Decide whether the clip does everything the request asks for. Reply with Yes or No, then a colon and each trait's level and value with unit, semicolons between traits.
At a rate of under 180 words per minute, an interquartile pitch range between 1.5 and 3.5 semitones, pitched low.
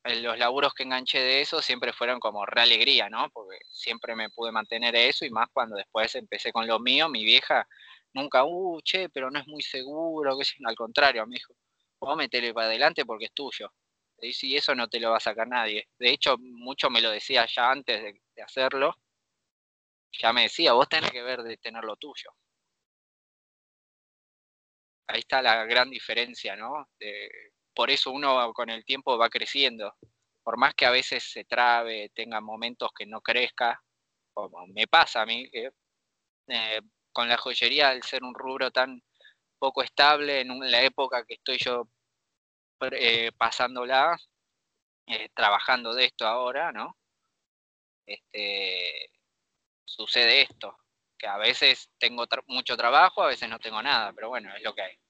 Yes: average, 170 wpm; average, 2.7 semitones; low, 120 Hz